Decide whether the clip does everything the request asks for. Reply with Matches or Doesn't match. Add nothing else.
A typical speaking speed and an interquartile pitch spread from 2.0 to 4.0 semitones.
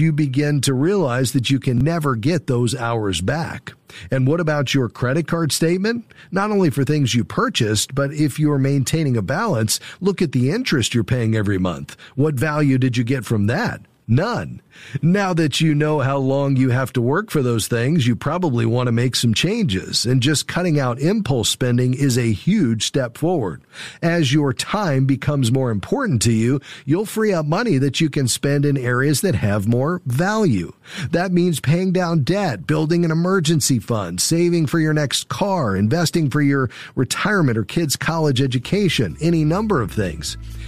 Doesn't match